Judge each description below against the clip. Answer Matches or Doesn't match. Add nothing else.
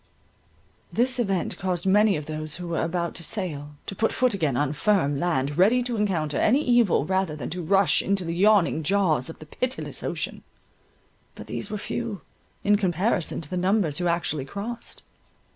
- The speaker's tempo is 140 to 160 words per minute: Doesn't match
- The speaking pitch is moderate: Matches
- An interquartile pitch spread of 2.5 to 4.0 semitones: Doesn't match